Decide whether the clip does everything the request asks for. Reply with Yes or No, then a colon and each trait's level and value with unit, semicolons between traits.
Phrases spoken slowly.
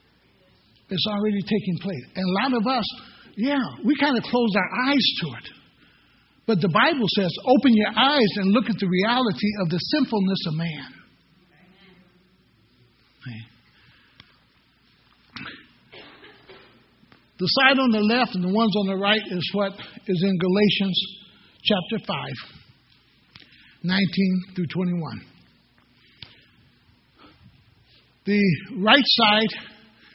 Yes: slow, 120 wpm